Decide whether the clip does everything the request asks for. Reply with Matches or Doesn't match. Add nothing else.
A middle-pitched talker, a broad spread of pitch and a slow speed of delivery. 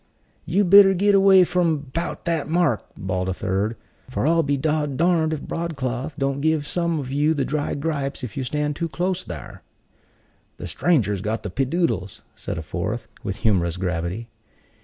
Doesn't match